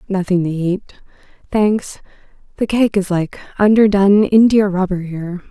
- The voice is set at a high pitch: Yes, high, 195 Hz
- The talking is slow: Yes, slow, 120 wpm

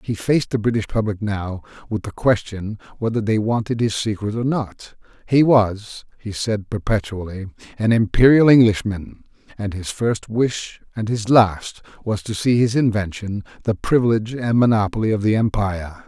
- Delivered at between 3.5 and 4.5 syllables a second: No, 4.9 syllables/s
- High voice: No, low, 110 Hz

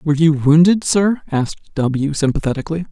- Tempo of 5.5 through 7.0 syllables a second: Yes, 5.8 syllables/s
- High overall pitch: No, medium, 160 Hz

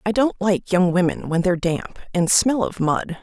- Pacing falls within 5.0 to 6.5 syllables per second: No, 4.7 syllables/s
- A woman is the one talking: Yes, female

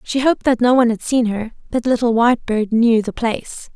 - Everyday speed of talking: No, fast, 225 wpm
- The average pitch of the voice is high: Yes, high, 235 Hz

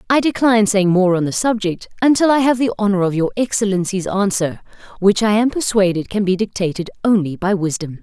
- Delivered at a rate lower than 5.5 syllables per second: No, 5.8 syllables/s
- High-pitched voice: Yes, high, 200 Hz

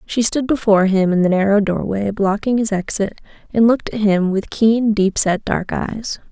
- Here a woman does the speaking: Yes, female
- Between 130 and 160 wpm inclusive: No, average, 200 wpm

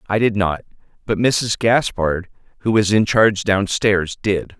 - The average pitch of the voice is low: Yes, low, 105 Hz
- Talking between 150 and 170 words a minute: Yes, average, 155 wpm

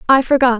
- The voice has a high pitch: Yes, very high, 255 Hz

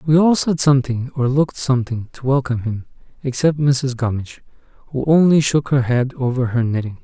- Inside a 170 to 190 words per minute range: Yes, average, 180 wpm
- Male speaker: Yes, male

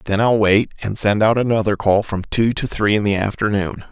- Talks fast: Yes, fast, 230 wpm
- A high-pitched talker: No, low, 105 Hz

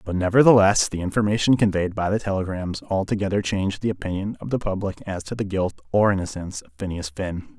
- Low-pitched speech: Yes, very low, 95 Hz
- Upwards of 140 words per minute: Yes, average, 190 wpm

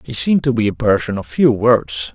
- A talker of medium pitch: No, low, 115 Hz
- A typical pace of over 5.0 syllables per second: Yes, 5.4 syllables/s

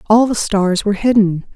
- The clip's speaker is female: Yes, female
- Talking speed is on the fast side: No, average, 195 wpm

